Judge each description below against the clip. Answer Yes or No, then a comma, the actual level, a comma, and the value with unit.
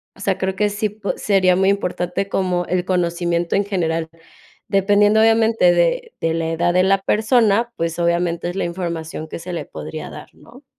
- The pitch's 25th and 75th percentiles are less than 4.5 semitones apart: Yes, average, 2.8 semitones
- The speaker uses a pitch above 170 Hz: Yes, medium, 185 Hz